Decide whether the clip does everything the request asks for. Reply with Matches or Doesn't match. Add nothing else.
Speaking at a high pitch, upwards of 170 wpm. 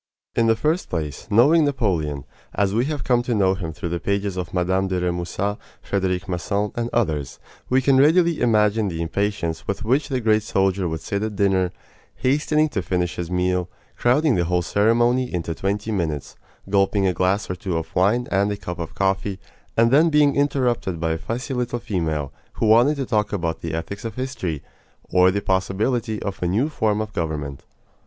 Doesn't match